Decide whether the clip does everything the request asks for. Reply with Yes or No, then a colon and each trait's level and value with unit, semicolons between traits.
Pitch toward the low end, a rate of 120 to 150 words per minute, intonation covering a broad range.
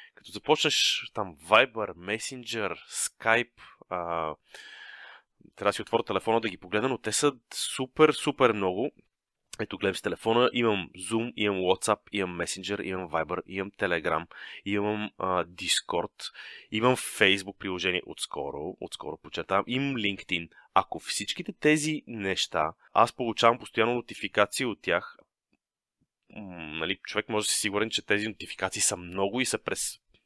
No: low, 105 Hz; average, 140 wpm; average, 3.6 semitones